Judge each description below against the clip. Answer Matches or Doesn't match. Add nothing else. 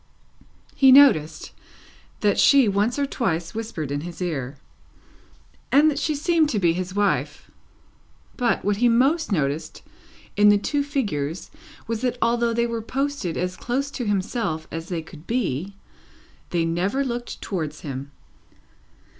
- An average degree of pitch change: Doesn't match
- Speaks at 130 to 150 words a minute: Matches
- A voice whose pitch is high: Matches